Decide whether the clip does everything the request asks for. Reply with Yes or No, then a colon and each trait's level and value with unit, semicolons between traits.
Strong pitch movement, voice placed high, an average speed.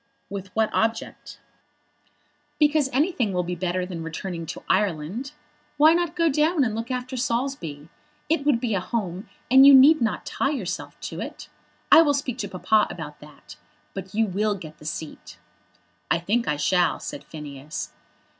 Yes: wide, 7.2 semitones; high, 220 Hz; average, 170 wpm